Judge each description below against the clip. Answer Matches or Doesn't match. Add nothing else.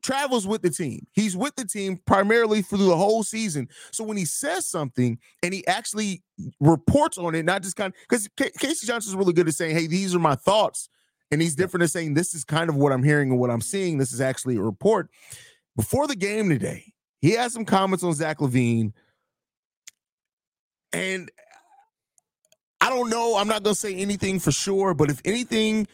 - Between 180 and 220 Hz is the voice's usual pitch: Matches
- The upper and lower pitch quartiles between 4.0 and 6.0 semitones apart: Matches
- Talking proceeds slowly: Doesn't match